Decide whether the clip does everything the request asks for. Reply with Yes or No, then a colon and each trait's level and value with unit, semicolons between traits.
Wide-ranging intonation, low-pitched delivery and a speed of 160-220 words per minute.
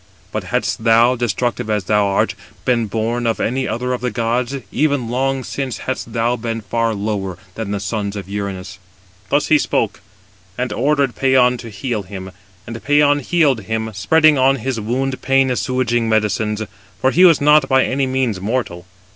No: average, 3.7 semitones; low, 120 Hz; average, 175 wpm